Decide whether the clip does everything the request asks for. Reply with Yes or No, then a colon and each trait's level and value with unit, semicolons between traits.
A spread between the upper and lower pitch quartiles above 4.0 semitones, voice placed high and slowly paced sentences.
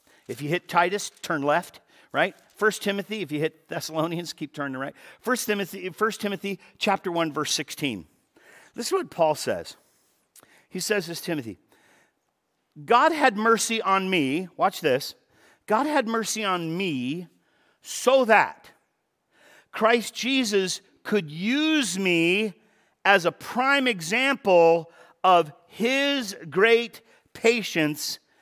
Yes: average, 5.2 semitones; high, 195 Hz; slow, 125 wpm